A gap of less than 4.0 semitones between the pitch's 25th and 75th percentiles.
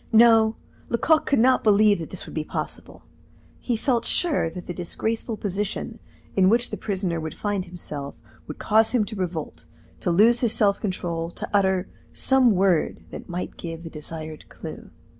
No: average, 4.6 semitones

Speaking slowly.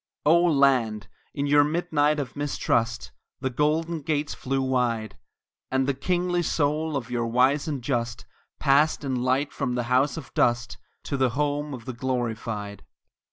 No: average, 160 wpm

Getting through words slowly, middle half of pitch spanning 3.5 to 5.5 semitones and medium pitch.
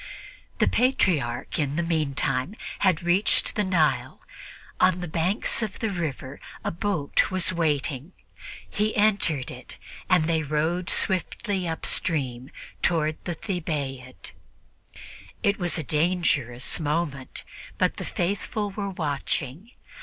Yes: slow, 120 wpm; average, 4.4 semitones; medium, 165 Hz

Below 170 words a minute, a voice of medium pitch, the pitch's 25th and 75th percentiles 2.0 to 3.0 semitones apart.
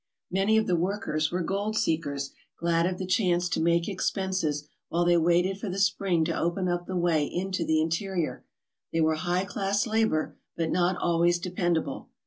No: average, 180 wpm; medium, 175 Hz; narrow, 2.4 semitones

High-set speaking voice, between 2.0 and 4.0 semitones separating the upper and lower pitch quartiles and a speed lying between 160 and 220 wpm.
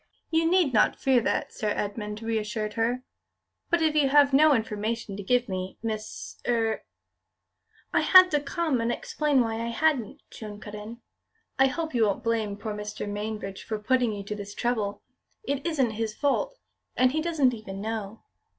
No: high, 230 Hz; average, 4.7 semitones; average, 180 wpm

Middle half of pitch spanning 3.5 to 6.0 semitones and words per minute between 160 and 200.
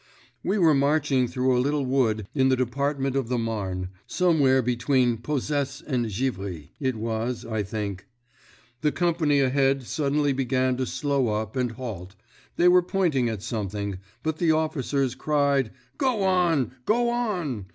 No: average, 4.5 semitones; average, 145 wpm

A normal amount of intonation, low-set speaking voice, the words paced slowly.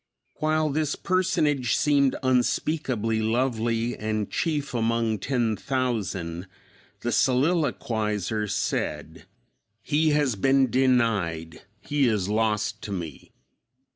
Yes: average, 4.5 semitones; low, 120 Hz; slow, 100 wpm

